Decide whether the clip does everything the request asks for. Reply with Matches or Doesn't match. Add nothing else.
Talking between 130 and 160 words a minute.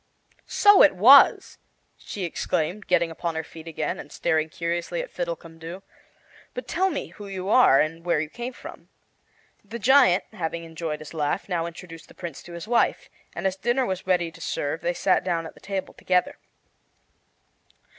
Doesn't match